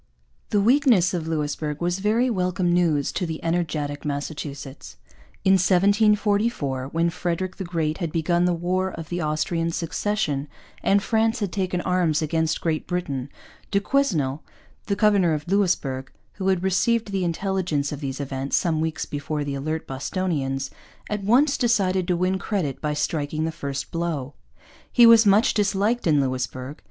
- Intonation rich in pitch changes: No, average, 4.6 semitones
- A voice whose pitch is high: No, medium, 170 Hz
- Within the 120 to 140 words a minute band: No, average, 155 wpm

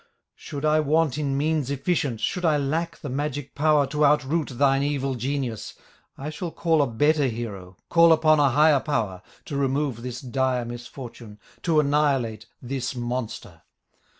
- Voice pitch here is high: No, medium, 140 Hz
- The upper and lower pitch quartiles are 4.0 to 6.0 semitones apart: No, average, 3.5 semitones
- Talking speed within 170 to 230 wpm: No, average, 155 wpm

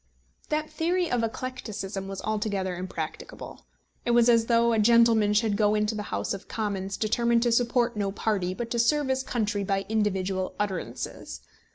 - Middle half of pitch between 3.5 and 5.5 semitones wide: No, average, 3.1 semitones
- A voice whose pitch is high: Yes, high, 215 Hz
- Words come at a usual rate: Yes, average, 170 wpm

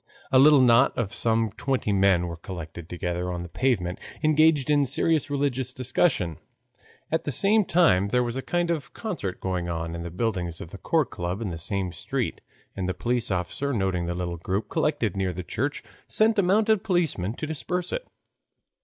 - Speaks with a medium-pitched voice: No, low, 115 Hz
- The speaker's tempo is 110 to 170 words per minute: No, average, 190 wpm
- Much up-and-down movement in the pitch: Yes, wide, 8.8 semitones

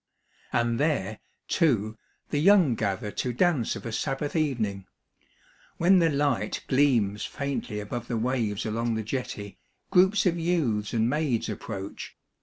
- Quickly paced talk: No, average, 140 wpm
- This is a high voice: No, low, 120 Hz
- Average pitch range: No, wide, 5.7 semitones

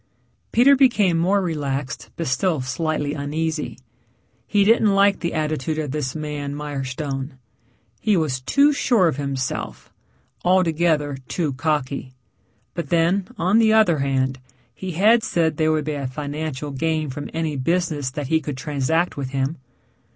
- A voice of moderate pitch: Yes, medium, 155 Hz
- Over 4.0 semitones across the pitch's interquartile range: No, average, 3.7 semitones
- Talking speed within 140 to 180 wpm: Yes, average, 150 wpm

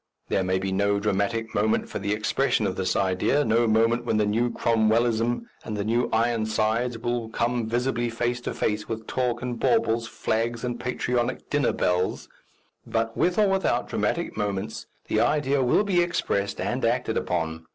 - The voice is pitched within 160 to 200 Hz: No, low, 115 Hz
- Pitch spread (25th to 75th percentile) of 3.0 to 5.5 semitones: No, narrow, 2.4 semitones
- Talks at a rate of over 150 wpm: Yes, average, 170 wpm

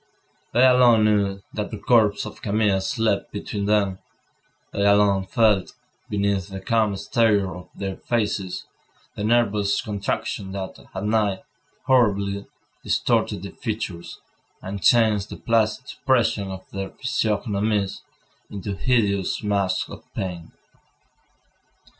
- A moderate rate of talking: No, slow, 120 wpm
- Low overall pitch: Yes, low, 100 Hz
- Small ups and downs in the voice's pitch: Yes, narrow, 2.1 semitones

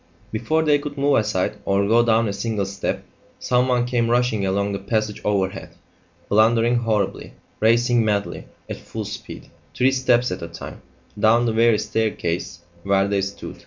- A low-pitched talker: Yes, low, 110 Hz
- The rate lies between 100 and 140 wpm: No, average, 165 wpm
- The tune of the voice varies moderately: Yes, average, 3.2 semitones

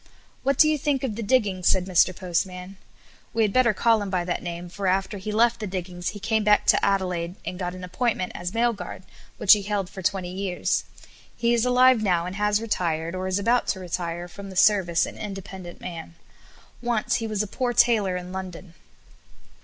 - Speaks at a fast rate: Yes, fast, 210 wpm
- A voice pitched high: Yes, high, 195 Hz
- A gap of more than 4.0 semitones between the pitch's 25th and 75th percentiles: No, average, 3.3 semitones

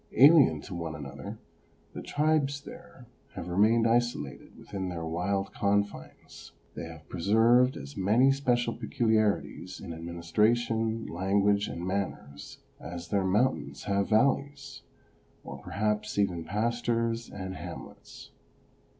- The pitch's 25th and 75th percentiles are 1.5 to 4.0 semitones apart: No, average, 4.8 semitones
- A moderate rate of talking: No, slow, 115 wpm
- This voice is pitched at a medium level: No, low, 105 Hz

